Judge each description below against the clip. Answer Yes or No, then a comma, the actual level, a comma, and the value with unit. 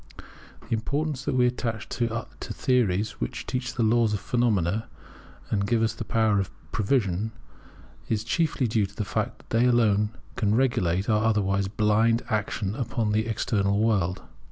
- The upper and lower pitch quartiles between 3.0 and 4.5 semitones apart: No, narrow, 2.5 semitones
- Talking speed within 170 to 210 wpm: No, average, 160 wpm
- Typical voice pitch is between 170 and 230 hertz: No, low, 110 Hz